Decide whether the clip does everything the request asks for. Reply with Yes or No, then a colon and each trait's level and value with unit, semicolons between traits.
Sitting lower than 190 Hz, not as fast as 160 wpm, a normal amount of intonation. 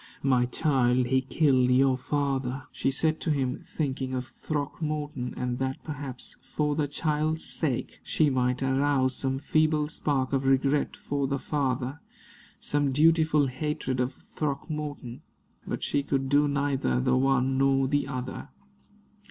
No: low, 135 Hz; average, 145 wpm; narrow, 2.2 semitones